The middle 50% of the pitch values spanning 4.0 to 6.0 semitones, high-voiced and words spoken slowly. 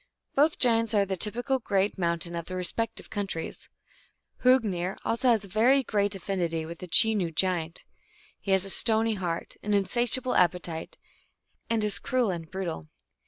No: average, 4.4 semitones; high, 200 Hz; average, 160 wpm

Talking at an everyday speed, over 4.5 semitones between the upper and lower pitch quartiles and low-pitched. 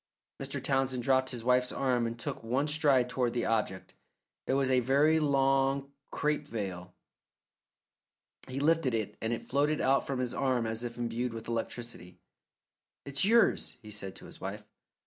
No: average, 165 wpm; average, 3.1 semitones; low, 125 Hz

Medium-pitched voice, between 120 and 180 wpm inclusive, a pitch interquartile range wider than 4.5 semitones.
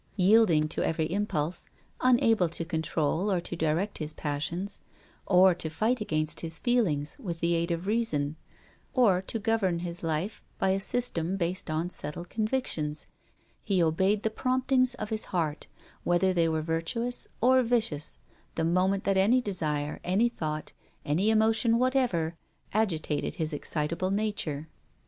Yes: medium, 180 Hz; average, 150 wpm; average, 5.3 semitones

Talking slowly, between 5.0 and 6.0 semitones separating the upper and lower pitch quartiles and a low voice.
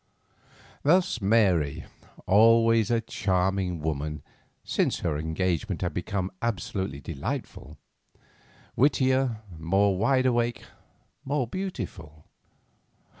Yes: slow, 80 wpm; average, 5.3 semitones; low, 100 Hz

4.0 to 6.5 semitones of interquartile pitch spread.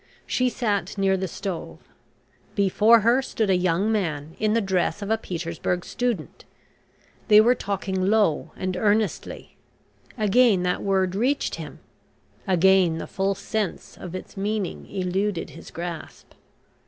No: average, 3.0 semitones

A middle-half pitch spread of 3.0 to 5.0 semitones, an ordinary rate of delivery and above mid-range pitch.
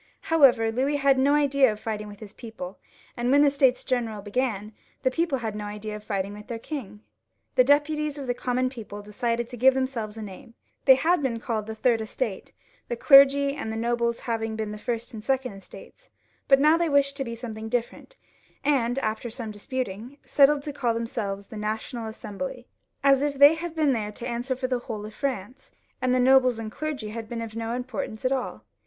No: average, 3.8 semitones; fast, 210 wpm; high, 240 Hz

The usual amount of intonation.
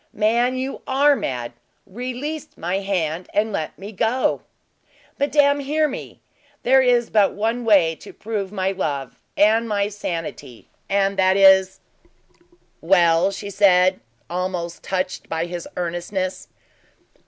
Yes: average, 4.8 semitones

